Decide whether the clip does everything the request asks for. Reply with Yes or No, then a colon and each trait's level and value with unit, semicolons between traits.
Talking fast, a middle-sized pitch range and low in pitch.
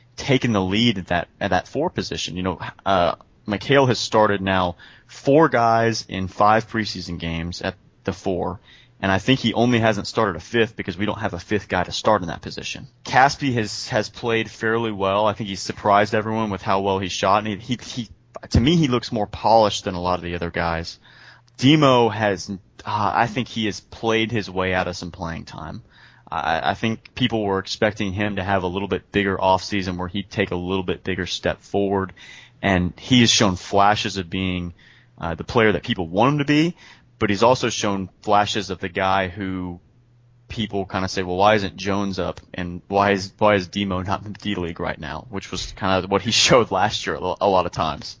Yes: fast, 220 wpm; average, 3.1 semitones; low, 100 Hz